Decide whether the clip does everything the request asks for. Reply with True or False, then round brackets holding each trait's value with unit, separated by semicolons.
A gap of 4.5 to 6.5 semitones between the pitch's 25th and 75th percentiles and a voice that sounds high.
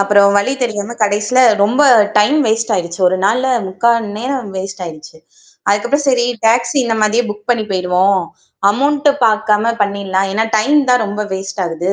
False (3.5 semitones; 210 Hz)